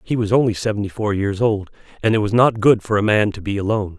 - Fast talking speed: Yes, fast, 270 wpm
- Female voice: No, male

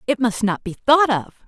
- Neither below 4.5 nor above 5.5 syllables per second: Yes, 5.2 syllables/s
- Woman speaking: Yes, female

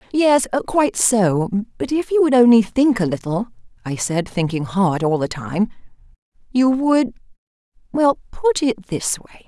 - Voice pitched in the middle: No, high, 220 Hz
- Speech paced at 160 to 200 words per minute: No, average, 150 wpm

